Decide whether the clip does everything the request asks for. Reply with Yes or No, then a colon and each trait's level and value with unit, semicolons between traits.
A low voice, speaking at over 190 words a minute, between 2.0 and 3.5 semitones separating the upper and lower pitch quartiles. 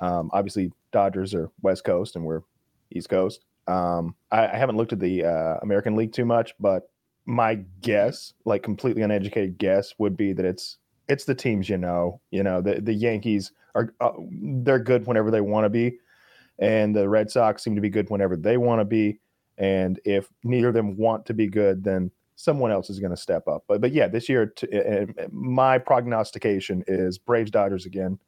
Yes: low, 100 Hz; average, 200 wpm; average, 3.1 semitones